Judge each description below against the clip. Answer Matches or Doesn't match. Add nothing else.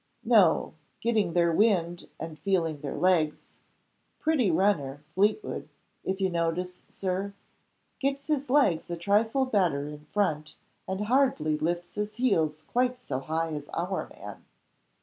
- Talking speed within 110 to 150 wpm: Matches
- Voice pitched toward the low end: Doesn't match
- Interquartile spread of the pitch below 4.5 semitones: Doesn't match